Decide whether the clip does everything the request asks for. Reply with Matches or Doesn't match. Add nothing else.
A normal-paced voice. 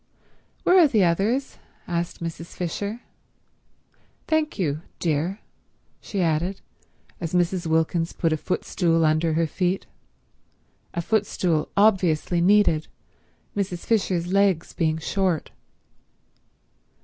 Doesn't match